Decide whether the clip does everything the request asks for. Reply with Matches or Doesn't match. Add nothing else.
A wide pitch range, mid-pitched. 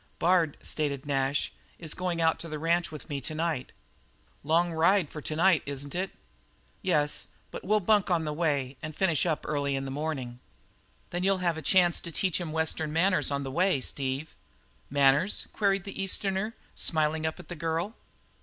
Doesn't match